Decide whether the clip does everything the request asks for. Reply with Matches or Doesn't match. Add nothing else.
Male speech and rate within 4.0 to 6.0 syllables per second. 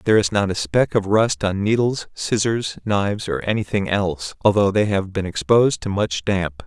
Matches